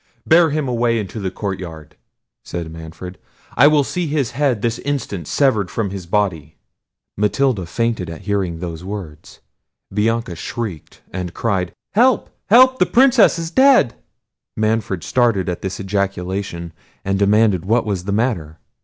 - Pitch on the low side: Yes, low, 100 Hz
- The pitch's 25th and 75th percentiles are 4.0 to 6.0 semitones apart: Yes, average, 5.2 semitones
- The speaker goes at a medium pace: Yes, average, 145 wpm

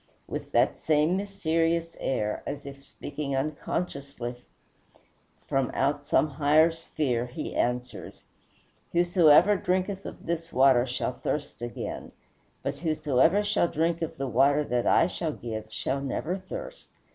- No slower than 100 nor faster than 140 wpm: Yes, slow, 135 wpm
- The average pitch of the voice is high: No, medium, 150 Hz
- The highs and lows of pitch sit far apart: No, average, 4.1 semitones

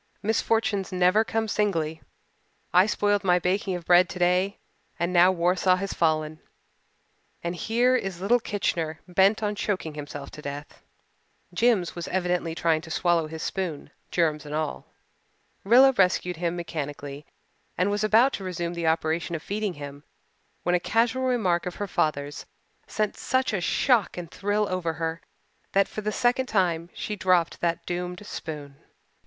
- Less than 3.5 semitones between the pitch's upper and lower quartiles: No, average, 3.9 semitones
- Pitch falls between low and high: Yes, medium, 180 Hz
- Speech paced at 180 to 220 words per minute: No, average, 160 wpm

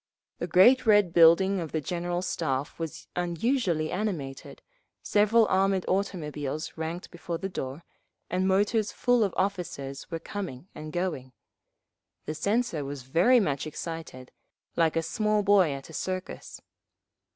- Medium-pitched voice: Yes, medium, 175 Hz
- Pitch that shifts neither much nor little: Yes, average, 4.3 semitones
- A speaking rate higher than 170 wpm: No, average, 140 wpm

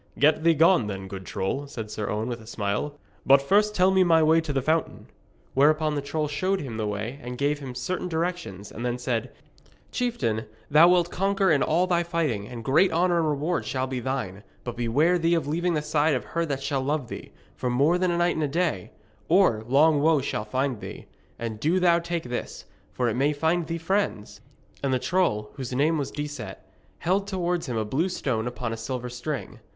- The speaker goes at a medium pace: No, fast, 215 wpm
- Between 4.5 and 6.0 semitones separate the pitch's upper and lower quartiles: Yes, wide, 5.5 semitones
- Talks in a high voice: No, medium, 145 Hz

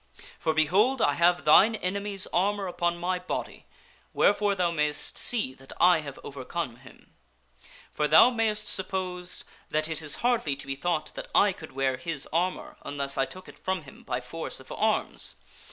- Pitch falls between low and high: Yes, medium, 170 Hz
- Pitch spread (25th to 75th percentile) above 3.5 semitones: Yes, average, 4.5 semitones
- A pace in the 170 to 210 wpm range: Yes, average, 175 wpm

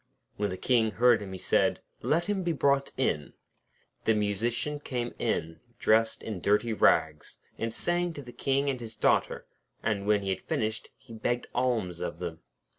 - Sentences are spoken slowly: No, average, 180 wpm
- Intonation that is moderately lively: Yes, average, 4.4 semitones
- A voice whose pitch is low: Yes, low, 115 Hz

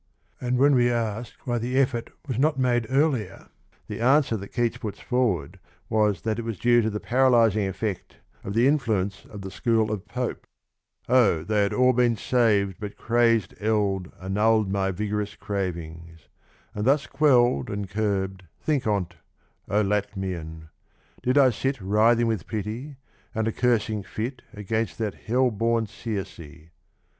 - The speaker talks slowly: No, average, 160 wpm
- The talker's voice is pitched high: No, low, 110 Hz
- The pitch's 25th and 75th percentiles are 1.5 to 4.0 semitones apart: Yes, average, 3.5 semitones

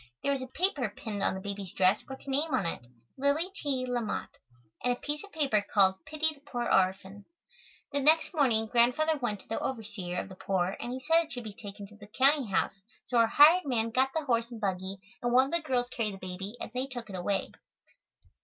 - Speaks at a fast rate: Yes, fast, 230 wpm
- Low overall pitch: No, high, 240 Hz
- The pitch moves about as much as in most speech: No, wide, 5.7 semitones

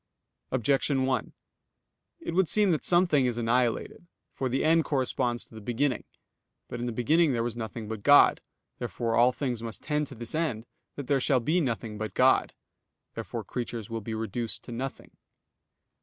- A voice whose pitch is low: Yes, low, 125 Hz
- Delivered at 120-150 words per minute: No, average, 175 wpm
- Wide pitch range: No, average, 3.8 semitones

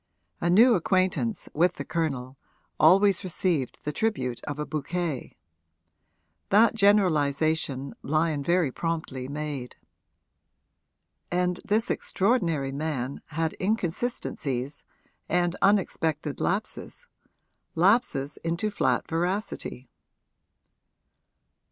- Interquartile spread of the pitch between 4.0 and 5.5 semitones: Yes, average, 5.0 semitones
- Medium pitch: Yes, medium, 165 Hz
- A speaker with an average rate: No, slow, 90 wpm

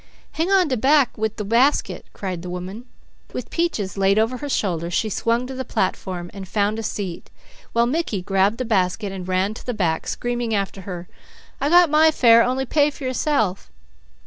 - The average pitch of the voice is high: Yes, high, 220 Hz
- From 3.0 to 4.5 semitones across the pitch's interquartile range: No, wide, 5.4 semitones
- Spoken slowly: No, average, 195 wpm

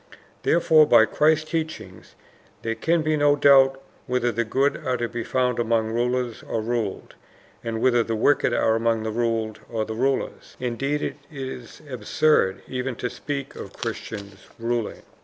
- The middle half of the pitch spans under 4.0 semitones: Yes, average, 3.5 semitones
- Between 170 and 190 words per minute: No, average, 160 wpm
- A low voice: Yes, low, 120 Hz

